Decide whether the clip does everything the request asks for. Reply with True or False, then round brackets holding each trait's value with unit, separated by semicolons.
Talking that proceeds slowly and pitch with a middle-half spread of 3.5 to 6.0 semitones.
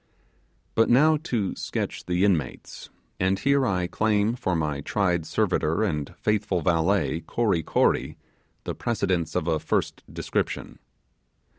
True (130 wpm; 4.7 semitones)